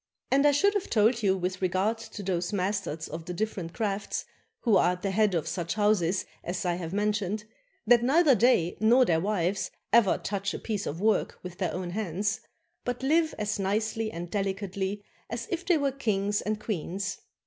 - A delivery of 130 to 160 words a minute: No, average, 195 wpm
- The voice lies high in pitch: Yes, high, 200 Hz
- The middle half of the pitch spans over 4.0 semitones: No, average, 3.3 semitones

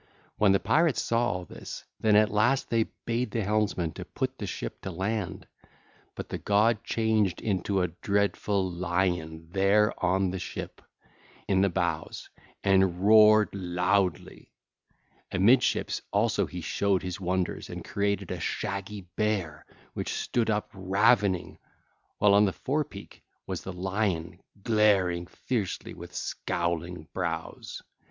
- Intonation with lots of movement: No, average, 2.8 semitones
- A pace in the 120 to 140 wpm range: Yes, slow, 135 wpm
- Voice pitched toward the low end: Yes, low, 100 Hz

